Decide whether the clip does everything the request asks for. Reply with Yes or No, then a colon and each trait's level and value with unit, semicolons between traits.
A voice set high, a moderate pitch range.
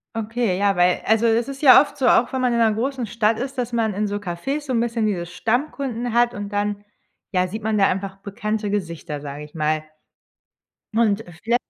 Yes: high, 220 Hz; average, 3.4 semitones